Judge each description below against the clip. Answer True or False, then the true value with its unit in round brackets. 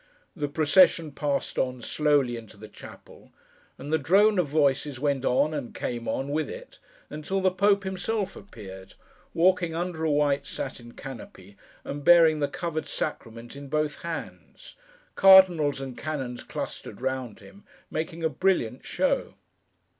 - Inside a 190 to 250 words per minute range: False (145 wpm)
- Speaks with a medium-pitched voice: True (150 Hz)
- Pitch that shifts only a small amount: False (4.7 semitones)